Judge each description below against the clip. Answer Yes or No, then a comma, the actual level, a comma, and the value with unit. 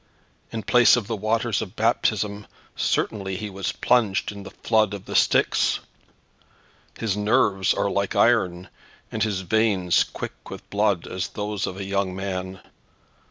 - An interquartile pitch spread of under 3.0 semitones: Yes, narrow, 2.4 semitones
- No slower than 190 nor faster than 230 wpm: No, average, 155 wpm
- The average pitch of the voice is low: Yes, low, 100 Hz